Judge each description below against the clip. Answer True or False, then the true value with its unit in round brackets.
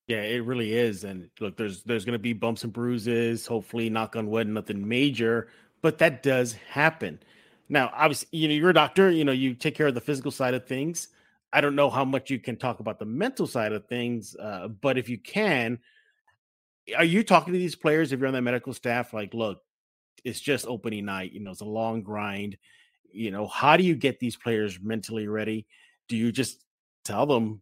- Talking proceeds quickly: True (215 wpm)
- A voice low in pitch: True (120 Hz)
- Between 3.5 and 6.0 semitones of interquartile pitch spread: True (4.3 semitones)